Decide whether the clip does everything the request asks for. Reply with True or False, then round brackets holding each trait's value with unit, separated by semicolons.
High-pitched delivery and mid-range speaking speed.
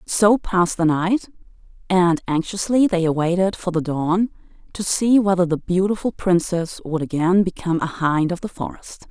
False (180 Hz; 165 wpm)